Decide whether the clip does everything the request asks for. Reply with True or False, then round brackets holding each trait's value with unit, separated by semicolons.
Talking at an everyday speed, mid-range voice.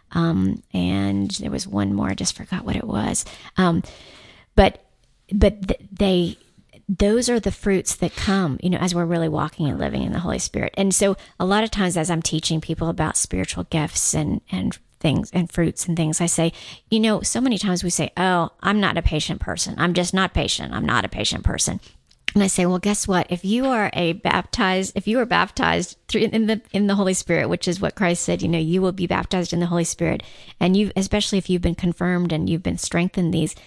False (230 wpm; 180 Hz)